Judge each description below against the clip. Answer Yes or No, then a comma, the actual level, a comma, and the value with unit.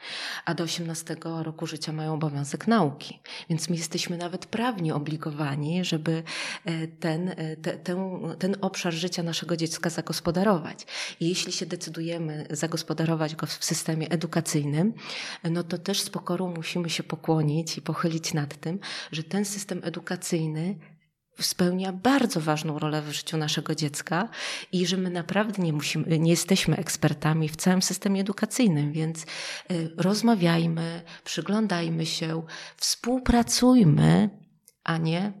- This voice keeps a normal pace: Yes, average, 130 wpm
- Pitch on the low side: No, medium, 170 Hz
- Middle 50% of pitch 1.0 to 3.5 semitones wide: Yes, narrow, 2.4 semitones